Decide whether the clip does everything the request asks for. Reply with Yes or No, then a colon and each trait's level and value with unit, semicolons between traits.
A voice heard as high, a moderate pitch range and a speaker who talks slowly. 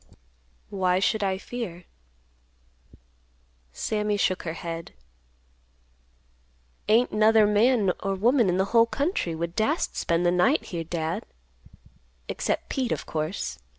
Yes: high, 195 Hz; average, 4.5 semitones; slow, 120 wpm